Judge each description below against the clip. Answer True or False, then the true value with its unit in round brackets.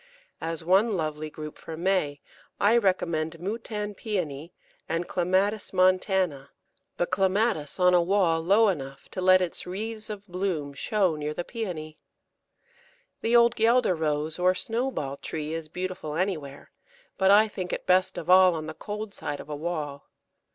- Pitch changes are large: False (4.3 semitones)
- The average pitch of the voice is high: False (180 Hz)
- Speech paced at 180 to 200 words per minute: False (160 wpm)